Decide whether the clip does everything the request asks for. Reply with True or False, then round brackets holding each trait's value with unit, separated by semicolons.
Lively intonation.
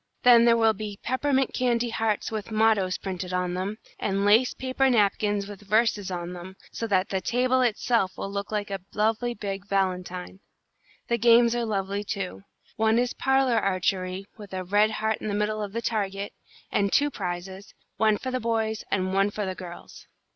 False (3.1 semitones)